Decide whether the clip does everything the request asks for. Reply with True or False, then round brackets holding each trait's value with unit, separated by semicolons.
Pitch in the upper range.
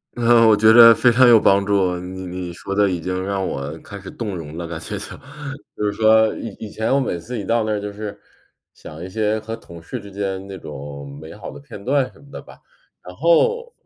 False (100 Hz)